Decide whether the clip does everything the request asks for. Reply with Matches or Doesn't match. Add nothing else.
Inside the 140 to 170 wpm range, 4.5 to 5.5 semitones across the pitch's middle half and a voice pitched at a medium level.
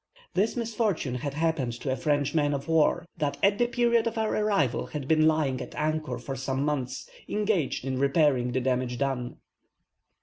Doesn't match